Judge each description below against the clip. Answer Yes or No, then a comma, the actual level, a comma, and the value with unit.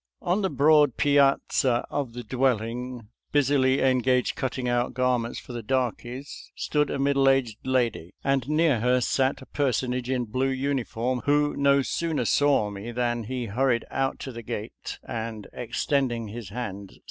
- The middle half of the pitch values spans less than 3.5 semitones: Yes, narrow, 2.5 semitones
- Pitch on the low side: Yes, low, 125 Hz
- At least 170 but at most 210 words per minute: Yes, average, 175 wpm